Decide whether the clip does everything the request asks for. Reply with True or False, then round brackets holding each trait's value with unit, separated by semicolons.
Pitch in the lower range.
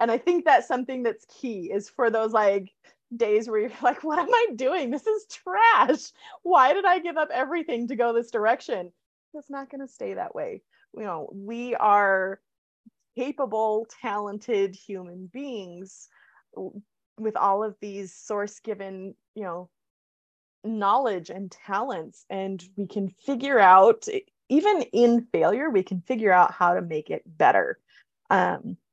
False (220 Hz)